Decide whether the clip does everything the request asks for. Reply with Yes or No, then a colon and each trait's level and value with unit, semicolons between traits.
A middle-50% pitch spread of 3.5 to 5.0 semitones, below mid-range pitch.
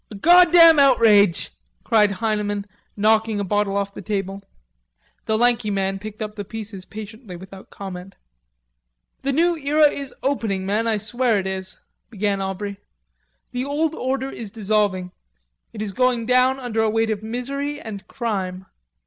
No: average, 4.1 semitones; high, 215 Hz